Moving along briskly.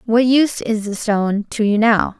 Yes: fast, 220 wpm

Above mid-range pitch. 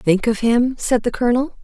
Yes: high, 235 Hz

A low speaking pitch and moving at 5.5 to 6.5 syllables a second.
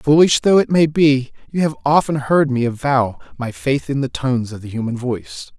No: low, 130 Hz; 5.1 syllables/s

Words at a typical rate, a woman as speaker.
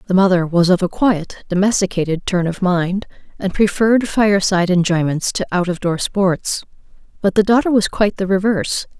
Yes: average, 180 wpm; female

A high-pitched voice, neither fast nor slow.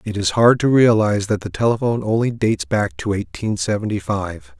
No: low, 110 Hz; average, 195 wpm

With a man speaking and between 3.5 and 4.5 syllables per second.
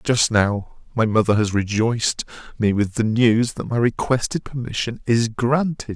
Yes: male; 4.4 syllables/s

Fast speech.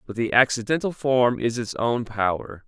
No: average, 180 wpm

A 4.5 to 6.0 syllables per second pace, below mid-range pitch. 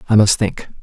Yes: 5.5 syllables/s; low, 105 Hz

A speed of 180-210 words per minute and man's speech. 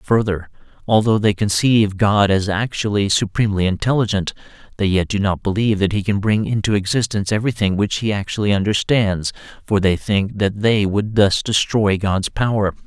No: average, 165 wpm; male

